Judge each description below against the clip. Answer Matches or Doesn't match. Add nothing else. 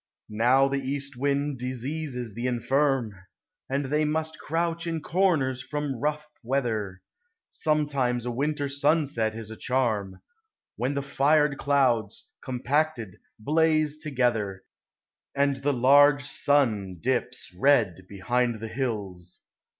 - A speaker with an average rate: Doesn't match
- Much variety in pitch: Doesn't match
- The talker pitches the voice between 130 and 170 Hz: Matches